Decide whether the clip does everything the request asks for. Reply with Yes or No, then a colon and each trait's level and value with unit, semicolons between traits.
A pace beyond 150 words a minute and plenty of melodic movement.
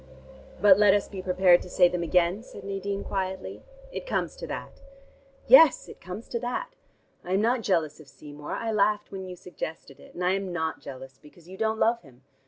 No: fast, 205 wpm; average, 3.3 semitones